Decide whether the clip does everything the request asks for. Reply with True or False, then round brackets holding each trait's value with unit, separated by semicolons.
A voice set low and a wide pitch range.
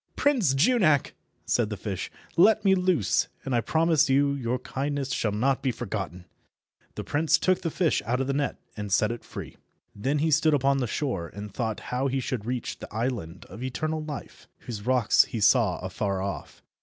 True (130 Hz; 5.7 semitones)